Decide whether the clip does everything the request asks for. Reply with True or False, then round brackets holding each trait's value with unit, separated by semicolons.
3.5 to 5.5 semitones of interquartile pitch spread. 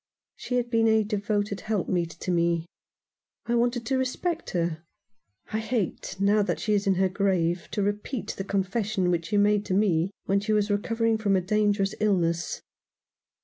False (2.8 semitones)